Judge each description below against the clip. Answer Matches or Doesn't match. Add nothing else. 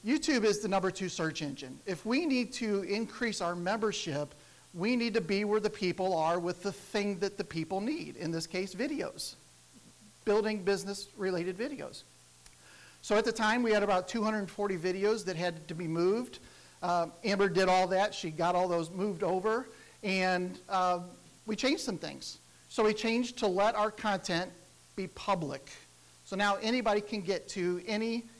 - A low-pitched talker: Doesn't match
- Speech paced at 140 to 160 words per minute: Doesn't match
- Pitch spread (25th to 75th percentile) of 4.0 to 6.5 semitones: Doesn't match